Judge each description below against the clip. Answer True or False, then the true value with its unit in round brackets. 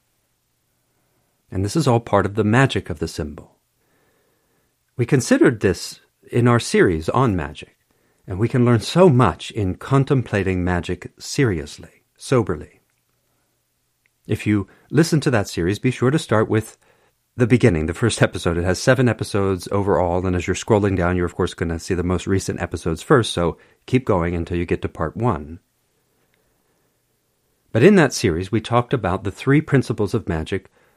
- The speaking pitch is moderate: False (105 Hz)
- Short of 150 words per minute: False (170 wpm)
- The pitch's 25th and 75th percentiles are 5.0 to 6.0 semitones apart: True (5.5 semitones)